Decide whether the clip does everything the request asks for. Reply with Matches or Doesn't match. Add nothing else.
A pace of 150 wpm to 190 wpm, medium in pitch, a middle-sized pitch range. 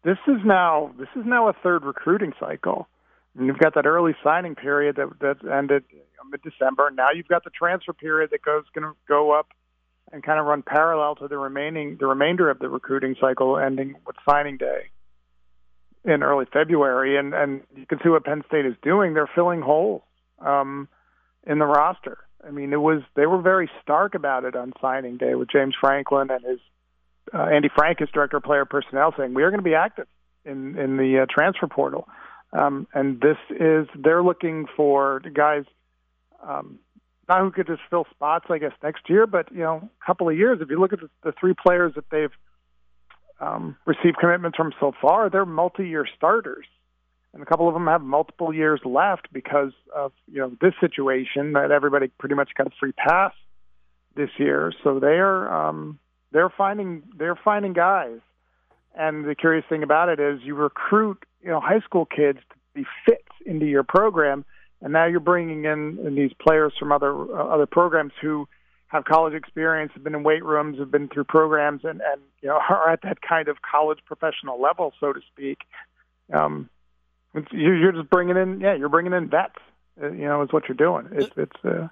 Doesn't match